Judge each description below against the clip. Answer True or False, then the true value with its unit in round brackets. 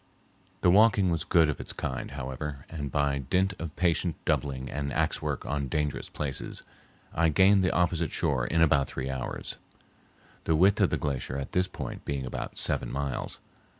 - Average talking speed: True (180 wpm)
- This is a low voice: True (75 Hz)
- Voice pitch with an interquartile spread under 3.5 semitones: False (3.8 semitones)